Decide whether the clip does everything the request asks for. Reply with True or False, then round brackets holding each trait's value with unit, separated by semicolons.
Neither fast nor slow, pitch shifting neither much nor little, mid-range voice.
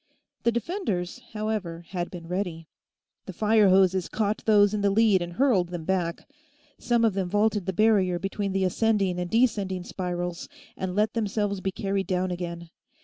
False (170 wpm; 3.1 semitones; 195 Hz)